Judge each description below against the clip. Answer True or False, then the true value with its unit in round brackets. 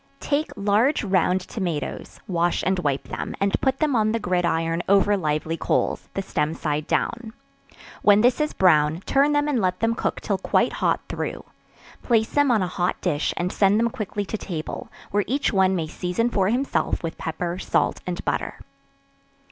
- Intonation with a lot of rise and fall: False (4.8 semitones)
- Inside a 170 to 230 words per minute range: True (180 wpm)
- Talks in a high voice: True (195 Hz)